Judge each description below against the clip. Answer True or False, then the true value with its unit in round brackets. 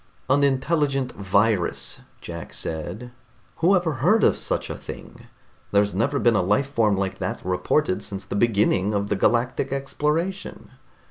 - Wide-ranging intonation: True (6.1 semitones)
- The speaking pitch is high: False (115 Hz)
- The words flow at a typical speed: True (150 wpm)